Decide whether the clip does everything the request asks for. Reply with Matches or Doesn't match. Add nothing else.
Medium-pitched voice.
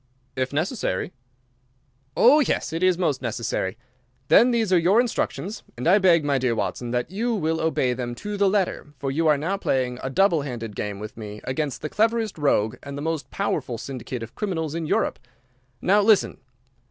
Matches